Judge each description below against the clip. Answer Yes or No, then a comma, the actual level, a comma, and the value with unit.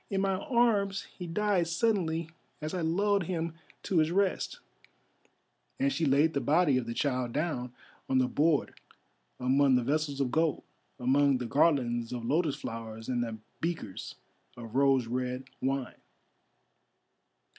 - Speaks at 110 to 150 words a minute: Yes, average, 145 wpm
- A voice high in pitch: No, medium, 145 Hz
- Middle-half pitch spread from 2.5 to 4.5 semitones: No, wide, 5.5 semitones